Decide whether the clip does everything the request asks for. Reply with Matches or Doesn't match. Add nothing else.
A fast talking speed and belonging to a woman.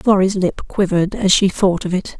Matches